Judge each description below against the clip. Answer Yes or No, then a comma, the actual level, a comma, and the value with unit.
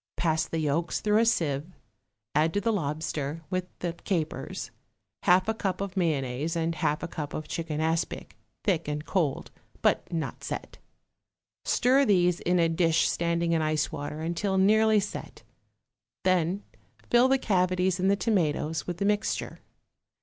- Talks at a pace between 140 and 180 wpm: Yes, average, 155 wpm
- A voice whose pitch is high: No, medium, 170 Hz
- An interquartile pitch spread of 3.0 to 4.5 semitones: Yes, average, 3.5 semitones